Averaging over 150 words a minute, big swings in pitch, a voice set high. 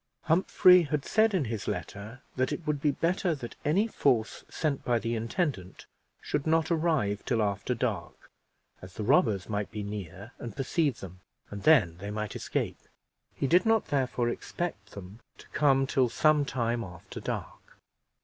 No: average, 170 wpm; wide, 6.9 semitones; low, 125 Hz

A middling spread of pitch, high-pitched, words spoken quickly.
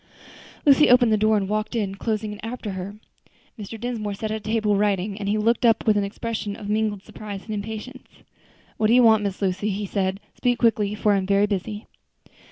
No: narrow, 1.7 semitones; high, 210 Hz; fast, 215 wpm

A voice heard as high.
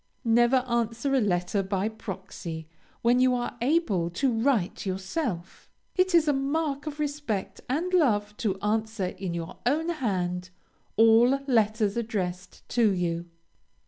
Yes: high, 225 Hz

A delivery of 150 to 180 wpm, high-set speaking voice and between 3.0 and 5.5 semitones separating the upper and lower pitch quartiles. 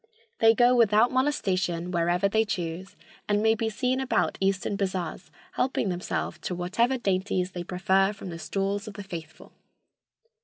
Yes: average, 155 wpm; high, 195 Hz; average, 3.6 semitones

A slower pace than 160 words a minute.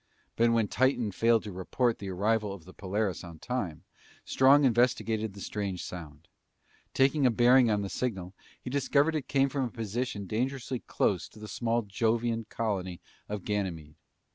No: average, 165 wpm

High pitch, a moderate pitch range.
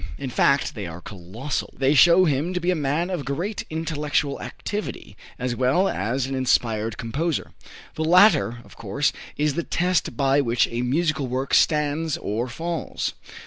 No: medium, 140 Hz; average, 4.8 semitones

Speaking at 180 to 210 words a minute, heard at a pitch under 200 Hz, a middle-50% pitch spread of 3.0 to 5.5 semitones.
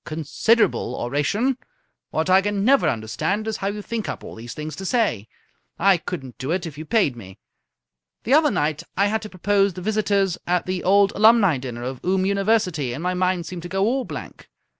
Yes: fast, 205 wpm; medium, 185 Hz; average, 5.2 semitones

